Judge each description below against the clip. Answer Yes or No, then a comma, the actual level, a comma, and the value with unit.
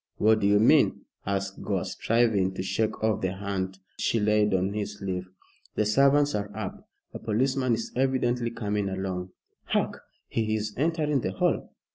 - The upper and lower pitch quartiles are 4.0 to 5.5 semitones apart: No, average, 3.2 semitones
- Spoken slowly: No, average, 165 wpm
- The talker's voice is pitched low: Yes, low, 105 Hz